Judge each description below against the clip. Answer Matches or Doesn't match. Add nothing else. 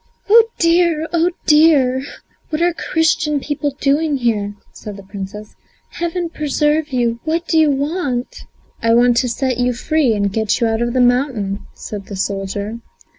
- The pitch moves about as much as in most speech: Doesn't match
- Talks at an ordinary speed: Matches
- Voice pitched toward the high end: Matches